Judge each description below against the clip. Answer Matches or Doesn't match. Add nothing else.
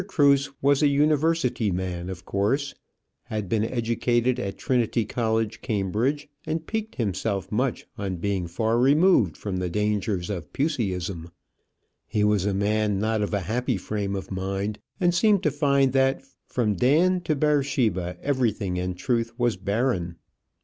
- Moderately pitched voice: Doesn't match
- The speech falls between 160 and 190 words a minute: Doesn't match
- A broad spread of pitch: Matches